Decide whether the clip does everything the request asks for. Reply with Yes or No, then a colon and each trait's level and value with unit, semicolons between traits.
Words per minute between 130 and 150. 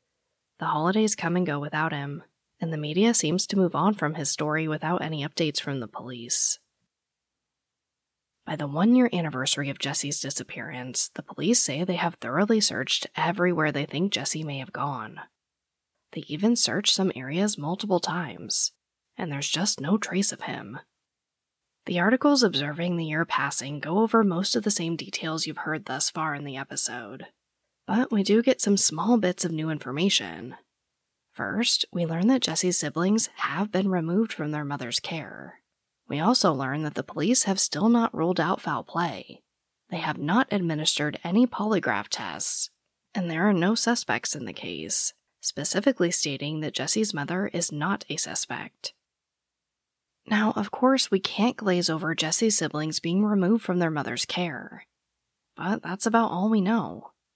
No: average, 165 wpm